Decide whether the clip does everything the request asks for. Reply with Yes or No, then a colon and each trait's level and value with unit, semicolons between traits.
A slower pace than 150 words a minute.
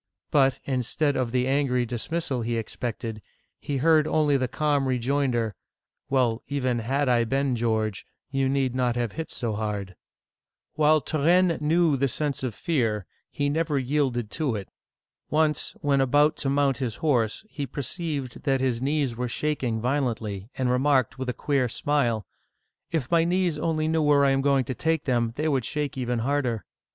No: average, 180 wpm